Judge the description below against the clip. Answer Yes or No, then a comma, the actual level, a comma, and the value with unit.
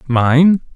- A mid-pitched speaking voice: Yes, medium, 145 Hz